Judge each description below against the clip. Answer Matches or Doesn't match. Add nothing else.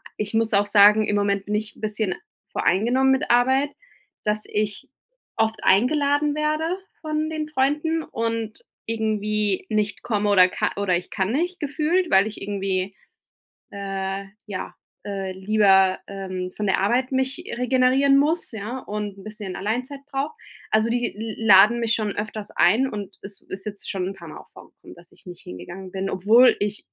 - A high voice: Matches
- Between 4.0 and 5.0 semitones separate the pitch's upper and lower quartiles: Matches